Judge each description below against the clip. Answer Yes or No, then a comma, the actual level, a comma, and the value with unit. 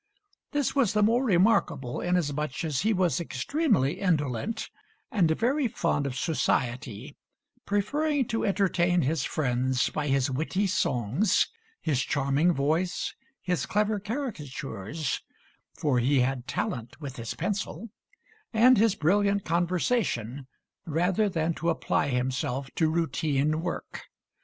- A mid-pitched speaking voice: Yes, medium, 165 Hz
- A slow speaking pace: Yes, slow, 125 wpm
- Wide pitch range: Yes, wide, 6.9 semitones